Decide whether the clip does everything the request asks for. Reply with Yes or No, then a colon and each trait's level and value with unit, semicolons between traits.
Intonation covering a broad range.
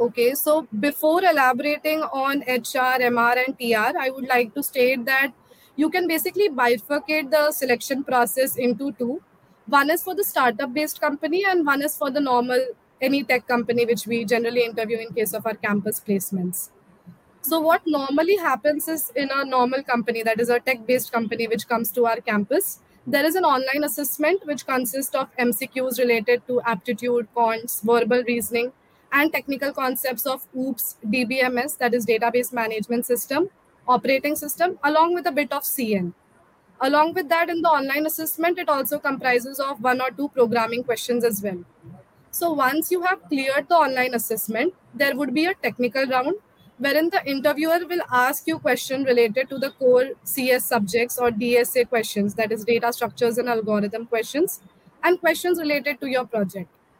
No: average, 3.8 semitones